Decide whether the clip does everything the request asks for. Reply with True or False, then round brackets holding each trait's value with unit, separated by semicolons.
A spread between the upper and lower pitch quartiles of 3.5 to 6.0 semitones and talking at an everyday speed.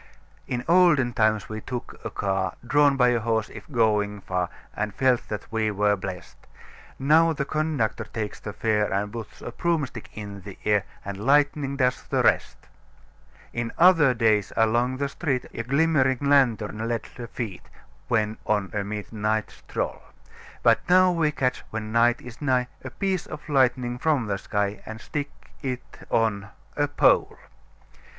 True (4.6 semitones; 160 wpm)